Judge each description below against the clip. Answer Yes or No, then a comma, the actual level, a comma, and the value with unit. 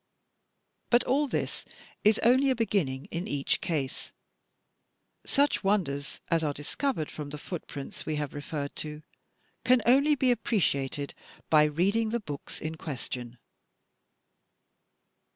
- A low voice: No, medium, 160 Hz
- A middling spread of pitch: No, wide, 8.3 semitones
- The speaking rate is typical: No, slow, 125 wpm